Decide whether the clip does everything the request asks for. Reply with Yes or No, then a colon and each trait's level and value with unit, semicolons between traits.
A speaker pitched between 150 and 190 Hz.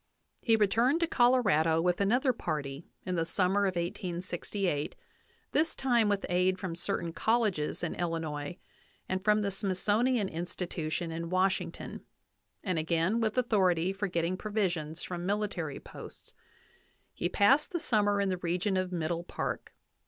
Yes: medium, 185 Hz